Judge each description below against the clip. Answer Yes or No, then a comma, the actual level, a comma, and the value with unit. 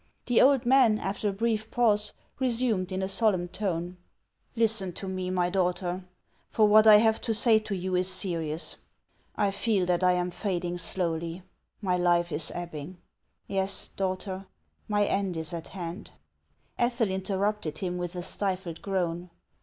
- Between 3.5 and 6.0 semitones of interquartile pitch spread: No, average, 3.0 semitones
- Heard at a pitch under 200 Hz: Yes, high, 190 Hz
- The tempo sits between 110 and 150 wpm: No, average, 160 wpm